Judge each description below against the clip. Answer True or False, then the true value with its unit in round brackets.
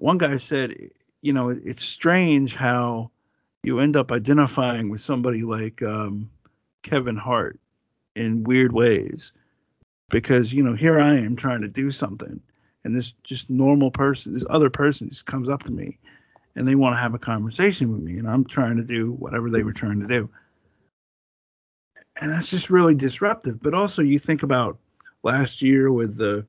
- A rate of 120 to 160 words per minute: False (175 wpm)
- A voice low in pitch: True (130 Hz)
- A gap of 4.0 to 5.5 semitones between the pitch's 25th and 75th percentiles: False (3.4 semitones)